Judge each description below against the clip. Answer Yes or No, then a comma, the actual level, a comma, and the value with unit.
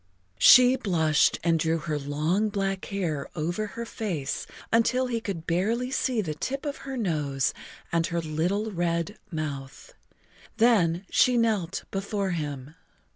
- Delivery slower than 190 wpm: Yes, average, 140 wpm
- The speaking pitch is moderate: Yes, medium, 180 Hz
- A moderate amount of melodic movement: No, wide, 5.8 semitones